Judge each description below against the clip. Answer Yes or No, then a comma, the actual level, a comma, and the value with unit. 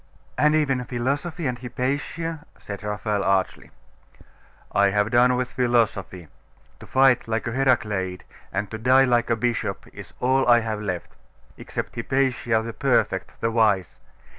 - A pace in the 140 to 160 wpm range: Yes, average, 145 wpm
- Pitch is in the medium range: No, low, 120 Hz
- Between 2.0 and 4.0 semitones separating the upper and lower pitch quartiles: Yes, average, 3.7 semitones